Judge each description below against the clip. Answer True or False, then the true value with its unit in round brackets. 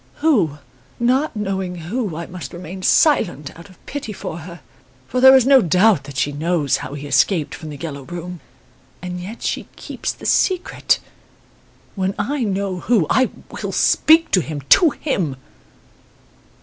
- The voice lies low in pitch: False (185 Hz)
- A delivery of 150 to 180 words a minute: True (160 wpm)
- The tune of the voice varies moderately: False (6.9 semitones)